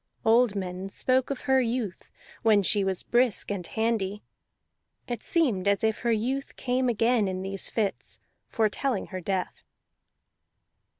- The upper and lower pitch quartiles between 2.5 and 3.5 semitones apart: No, average, 4.1 semitones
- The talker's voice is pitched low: No, high, 220 Hz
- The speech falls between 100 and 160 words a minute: Yes, average, 140 wpm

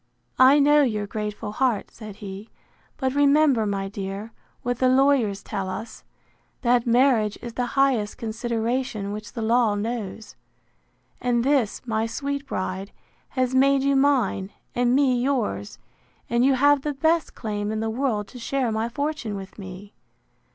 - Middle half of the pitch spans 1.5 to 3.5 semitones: No, average, 4.3 semitones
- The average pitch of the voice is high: Yes, high, 235 Hz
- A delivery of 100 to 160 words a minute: Yes, average, 155 wpm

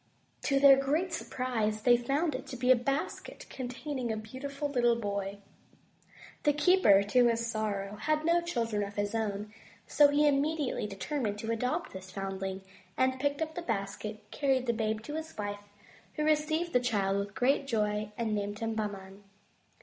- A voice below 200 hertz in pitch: No, high, 235 Hz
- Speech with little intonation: No, average, 5.3 semitones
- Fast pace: No, average, 175 wpm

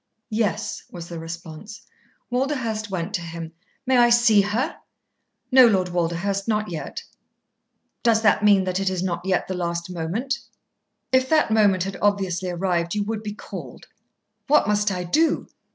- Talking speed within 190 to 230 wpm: No, average, 160 wpm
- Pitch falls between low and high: No, high, 195 Hz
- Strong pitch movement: No, average, 3.9 semitones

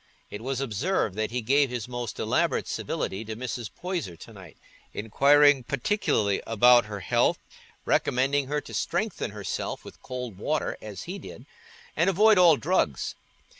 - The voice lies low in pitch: Yes, low, 125 Hz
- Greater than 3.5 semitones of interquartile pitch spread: Yes, average, 5.1 semitones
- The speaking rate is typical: Yes, average, 155 wpm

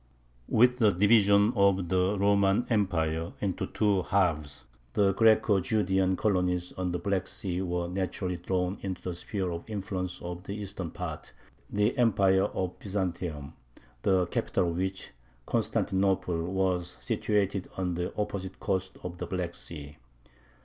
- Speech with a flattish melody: Yes, narrow, 2.1 semitones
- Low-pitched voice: Yes, very low, 95 Hz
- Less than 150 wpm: Yes, average, 140 wpm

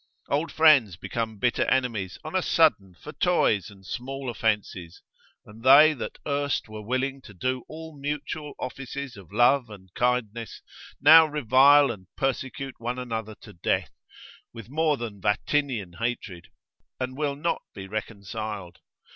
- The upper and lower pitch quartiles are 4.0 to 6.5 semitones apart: Yes, average, 5.0 semitones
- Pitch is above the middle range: No, low, 125 Hz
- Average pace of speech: Yes, average, 145 wpm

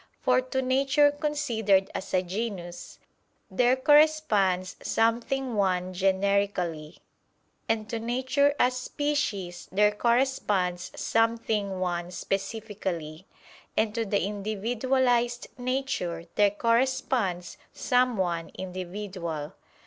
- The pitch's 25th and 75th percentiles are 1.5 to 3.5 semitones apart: No, average, 5.3 semitones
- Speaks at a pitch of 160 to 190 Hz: No, high, 210 Hz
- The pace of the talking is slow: Yes, slow, 95 wpm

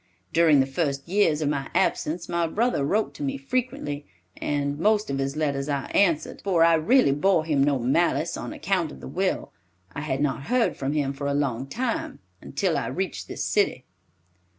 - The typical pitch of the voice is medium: Yes, medium, 150 Hz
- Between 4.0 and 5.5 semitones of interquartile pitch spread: Yes, average, 5.0 semitones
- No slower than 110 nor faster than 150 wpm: No, average, 195 wpm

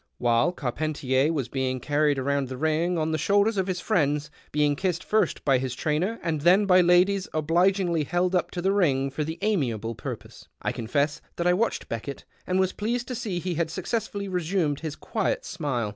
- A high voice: No, medium, 160 Hz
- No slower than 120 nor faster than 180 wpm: No, average, 195 wpm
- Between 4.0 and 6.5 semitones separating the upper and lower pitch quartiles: Yes, average, 4.7 semitones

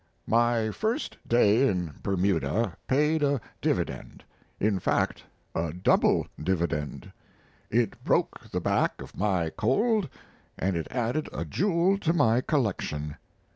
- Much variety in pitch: Yes, wide, 8.1 semitones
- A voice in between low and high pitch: No, low, 110 Hz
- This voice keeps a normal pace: No, slow, 125 wpm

